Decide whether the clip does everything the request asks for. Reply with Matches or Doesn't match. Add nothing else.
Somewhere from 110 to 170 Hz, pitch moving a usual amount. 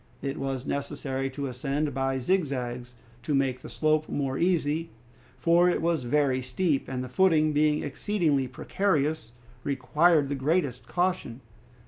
Matches